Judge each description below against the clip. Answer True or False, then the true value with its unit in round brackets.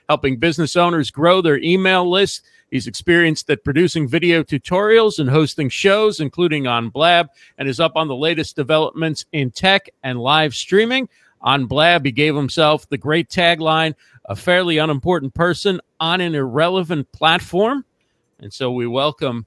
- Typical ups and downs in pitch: True (3.6 semitones)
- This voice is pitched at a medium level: True (160 Hz)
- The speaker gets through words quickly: False (155 wpm)